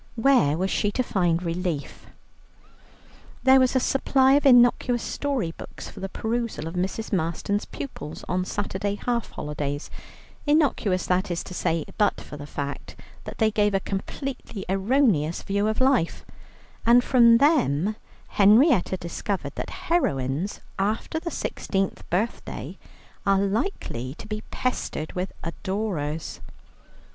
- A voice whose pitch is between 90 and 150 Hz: No, high, 200 Hz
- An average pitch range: No, wide, 6.0 semitones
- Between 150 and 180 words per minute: No, slow, 135 wpm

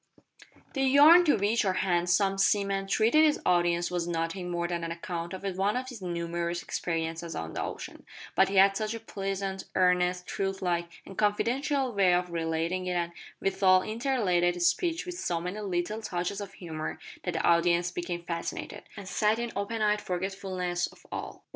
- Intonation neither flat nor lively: Yes, average, 3.1 semitones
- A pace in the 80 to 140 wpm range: No, average, 185 wpm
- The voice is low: No, medium, 185 Hz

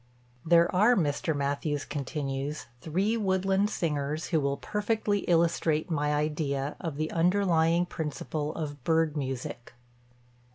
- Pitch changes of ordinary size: Yes, average, 3.3 semitones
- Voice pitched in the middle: Yes, medium, 155 Hz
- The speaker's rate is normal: No, slow, 120 wpm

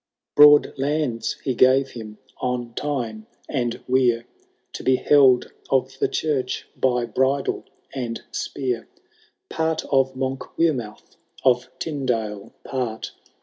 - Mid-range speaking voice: No, low, 130 Hz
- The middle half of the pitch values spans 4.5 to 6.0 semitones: No, narrow, 2.4 semitones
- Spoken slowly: Yes, slow, 120 wpm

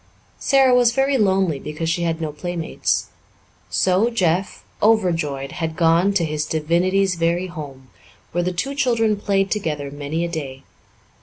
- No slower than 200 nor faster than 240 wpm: No, average, 150 wpm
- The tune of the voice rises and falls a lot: No, average, 4.1 semitones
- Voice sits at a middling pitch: Yes, medium, 170 Hz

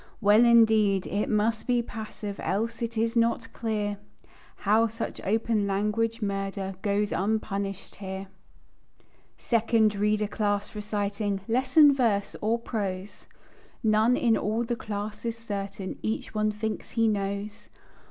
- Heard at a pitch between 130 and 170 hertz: No, high, 215 Hz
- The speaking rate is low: Yes, slow, 130 wpm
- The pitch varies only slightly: Yes, narrow, 2.1 semitones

